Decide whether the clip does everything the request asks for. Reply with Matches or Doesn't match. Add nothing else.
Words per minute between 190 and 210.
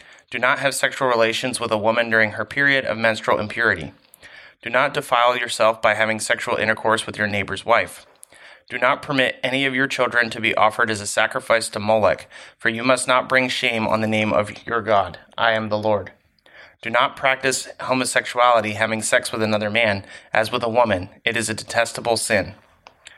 Matches